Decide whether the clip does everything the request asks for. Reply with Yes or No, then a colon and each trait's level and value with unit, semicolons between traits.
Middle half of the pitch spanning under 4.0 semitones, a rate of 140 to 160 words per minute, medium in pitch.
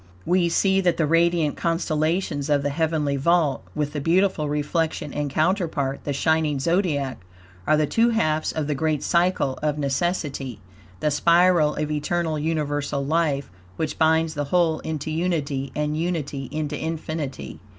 Yes: narrow, 2.5 semitones; average, 150 wpm; medium, 155 Hz